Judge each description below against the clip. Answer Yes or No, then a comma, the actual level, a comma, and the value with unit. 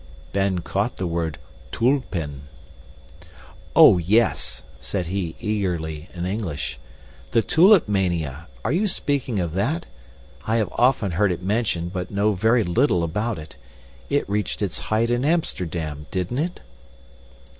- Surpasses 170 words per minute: No, slow, 135 wpm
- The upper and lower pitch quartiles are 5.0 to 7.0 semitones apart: Yes, average, 5.3 semitones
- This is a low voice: Yes, low, 100 Hz